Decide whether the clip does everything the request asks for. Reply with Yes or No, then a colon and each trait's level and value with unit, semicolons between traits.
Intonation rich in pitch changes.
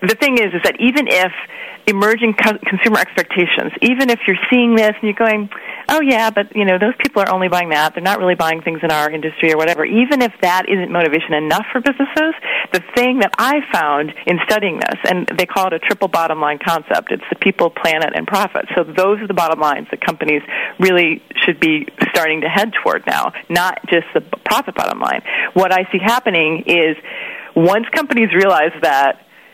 Yes: wide, 5.7 semitones